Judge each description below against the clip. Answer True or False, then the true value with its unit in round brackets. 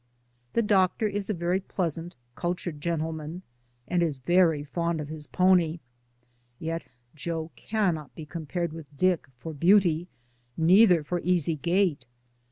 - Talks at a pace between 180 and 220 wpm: False (140 wpm)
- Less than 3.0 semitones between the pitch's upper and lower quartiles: True (2.5 semitones)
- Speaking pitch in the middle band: True (170 Hz)